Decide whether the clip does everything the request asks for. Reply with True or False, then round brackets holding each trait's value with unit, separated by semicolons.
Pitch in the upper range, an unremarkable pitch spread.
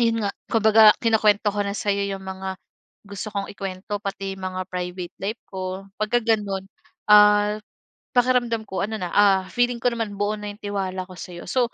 False (205 Hz; 2.2 semitones)